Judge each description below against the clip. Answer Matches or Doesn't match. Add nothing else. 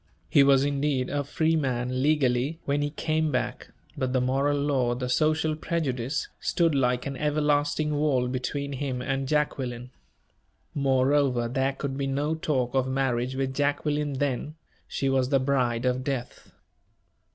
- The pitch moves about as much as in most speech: Doesn't match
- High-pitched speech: Doesn't match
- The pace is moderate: Matches